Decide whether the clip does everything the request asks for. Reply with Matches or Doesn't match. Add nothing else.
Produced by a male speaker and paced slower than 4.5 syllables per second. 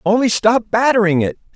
Doesn't match